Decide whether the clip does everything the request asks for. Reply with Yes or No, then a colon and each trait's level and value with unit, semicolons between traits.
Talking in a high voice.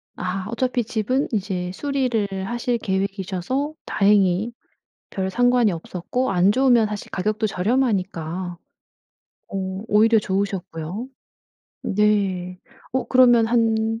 Yes: high, 210 Hz